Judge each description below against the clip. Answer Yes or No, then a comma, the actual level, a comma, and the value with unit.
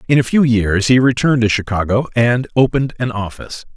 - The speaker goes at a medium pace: Yes, average, 190 wpm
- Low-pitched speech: Yes, low, 120 Hz